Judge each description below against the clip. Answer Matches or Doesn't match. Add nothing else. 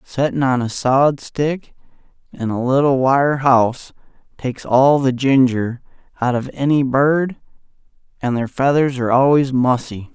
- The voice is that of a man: Matches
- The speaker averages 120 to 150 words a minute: Matches